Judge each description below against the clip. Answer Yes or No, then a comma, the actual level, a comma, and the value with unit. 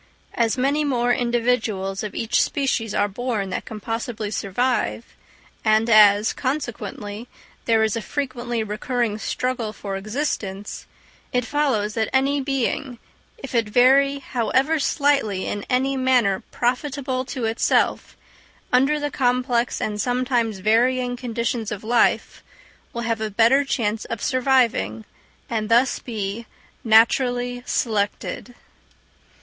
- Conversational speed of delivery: No, slow, 125 wpm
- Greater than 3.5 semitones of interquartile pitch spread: No, average, 3.0 semitones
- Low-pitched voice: No, high, 235 Hz